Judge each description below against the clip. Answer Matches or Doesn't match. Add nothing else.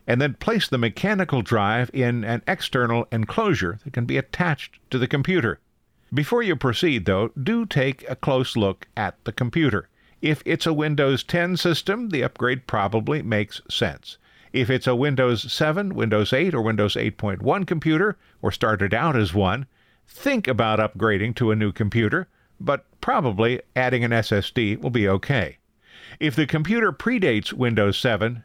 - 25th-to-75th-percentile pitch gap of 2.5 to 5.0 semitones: Doesn't match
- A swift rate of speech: Doesn't match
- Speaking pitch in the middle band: Doesn't match